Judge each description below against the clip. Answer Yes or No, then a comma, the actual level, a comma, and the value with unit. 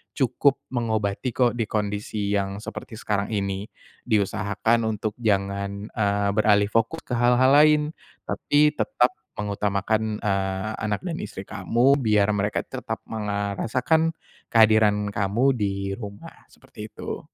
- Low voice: Yes, low, 105 Hz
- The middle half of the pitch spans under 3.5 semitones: Yes, average, 2.8 semitones